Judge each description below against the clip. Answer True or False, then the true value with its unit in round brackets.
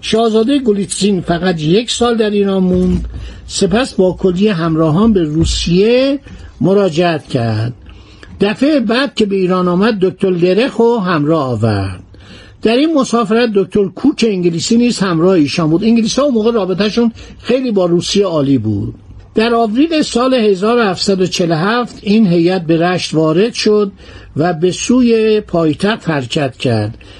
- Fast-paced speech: False (135 wpm)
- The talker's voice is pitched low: False (190 Hz)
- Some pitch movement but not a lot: False (5.7 semitones)